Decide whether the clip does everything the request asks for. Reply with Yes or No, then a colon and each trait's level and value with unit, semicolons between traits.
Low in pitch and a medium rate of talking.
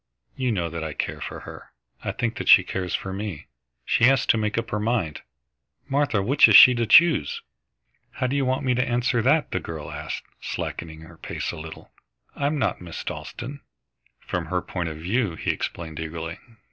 Yes: low, 105 Hz; average, 195 wpm